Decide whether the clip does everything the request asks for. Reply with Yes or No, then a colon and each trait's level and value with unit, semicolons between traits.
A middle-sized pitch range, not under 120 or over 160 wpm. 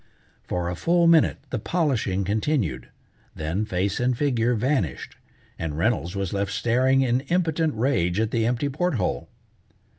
No: wide, 6.7 semitones; average, 150 wpm